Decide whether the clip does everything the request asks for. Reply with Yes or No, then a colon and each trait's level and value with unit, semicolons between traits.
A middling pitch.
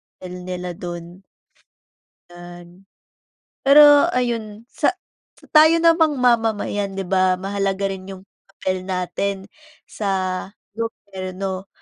No: high, 195 Hz